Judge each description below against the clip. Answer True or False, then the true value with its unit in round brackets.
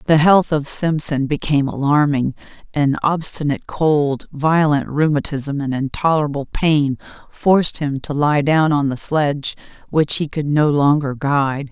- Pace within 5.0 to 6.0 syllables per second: False (4.5 syllables/s)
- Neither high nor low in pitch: True (145 Hz)